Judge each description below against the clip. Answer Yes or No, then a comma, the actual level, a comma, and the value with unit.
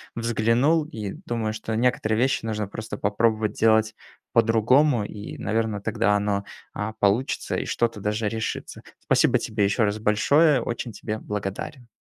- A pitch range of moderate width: No, narrow, 2.0 semitones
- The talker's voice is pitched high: No, low, 110 Hz